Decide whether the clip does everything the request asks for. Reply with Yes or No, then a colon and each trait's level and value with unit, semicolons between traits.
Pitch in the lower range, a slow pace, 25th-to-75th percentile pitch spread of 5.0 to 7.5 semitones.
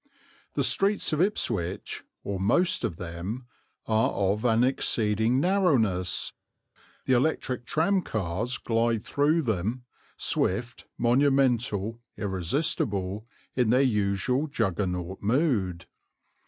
Yes: low, 115 Hz; slow, 100 wpm; average, 5.3 semitones